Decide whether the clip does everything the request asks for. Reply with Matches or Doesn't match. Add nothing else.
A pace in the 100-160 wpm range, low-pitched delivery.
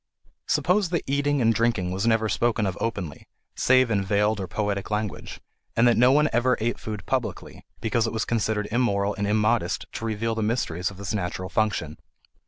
Doesn't match